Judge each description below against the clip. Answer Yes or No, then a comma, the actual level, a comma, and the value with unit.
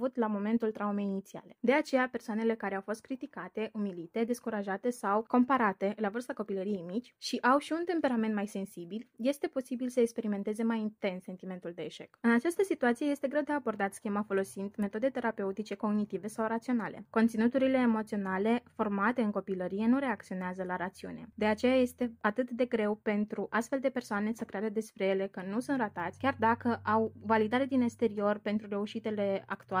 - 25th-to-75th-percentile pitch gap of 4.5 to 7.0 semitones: No, average, 3.3 semitones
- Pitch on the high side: Yes, high, 220 Hz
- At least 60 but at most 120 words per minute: No, fast, 170 wpm